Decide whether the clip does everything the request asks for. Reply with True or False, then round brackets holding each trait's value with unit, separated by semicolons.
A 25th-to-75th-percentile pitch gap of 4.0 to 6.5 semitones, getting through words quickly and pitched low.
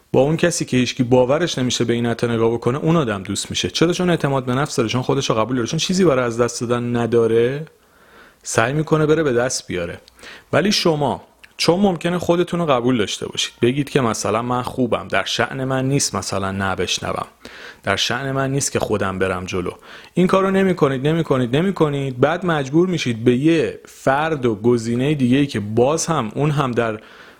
True (5.2 semitones; 195 wpm; 130 Hz)